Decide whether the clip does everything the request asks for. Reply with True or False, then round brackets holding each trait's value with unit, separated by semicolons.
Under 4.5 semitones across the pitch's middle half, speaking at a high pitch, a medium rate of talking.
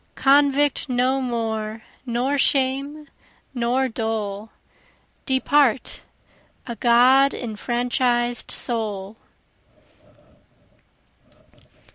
False (3.0 semitones; 245 Hz; 60 wpm)